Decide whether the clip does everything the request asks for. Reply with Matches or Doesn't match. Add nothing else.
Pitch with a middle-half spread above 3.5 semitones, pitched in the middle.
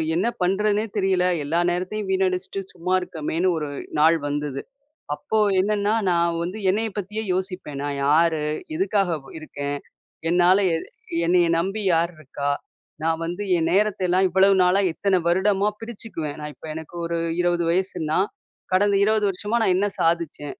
Doesn't match